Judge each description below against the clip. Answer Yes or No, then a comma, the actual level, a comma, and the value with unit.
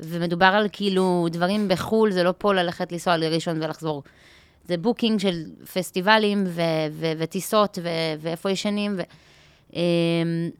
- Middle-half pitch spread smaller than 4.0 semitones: Yes, average, 2.9 semitones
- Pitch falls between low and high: Yes, medium, 175 Hz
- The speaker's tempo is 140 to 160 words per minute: No, average, 110 wpm